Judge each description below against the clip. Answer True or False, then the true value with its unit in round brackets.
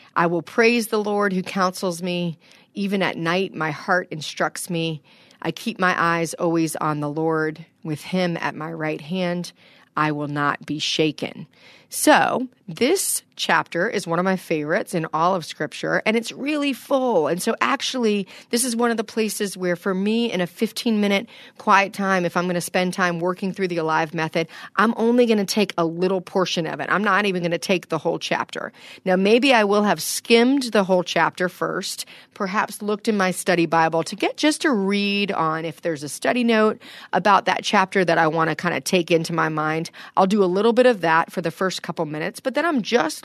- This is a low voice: False (185 Hz)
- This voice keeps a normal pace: False (215 wpm)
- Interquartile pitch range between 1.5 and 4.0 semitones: False (4.5 semitones)